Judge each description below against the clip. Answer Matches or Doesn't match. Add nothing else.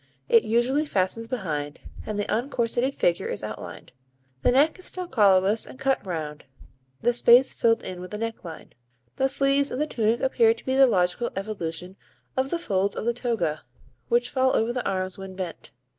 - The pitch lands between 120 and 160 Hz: Doesn't match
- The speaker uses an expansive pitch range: Matches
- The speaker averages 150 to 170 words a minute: Doesn't match